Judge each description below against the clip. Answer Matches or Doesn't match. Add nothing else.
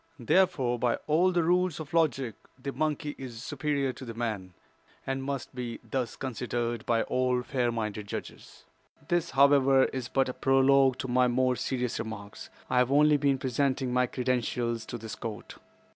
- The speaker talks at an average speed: Matches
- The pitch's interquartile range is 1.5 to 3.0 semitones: Matches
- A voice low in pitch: Matches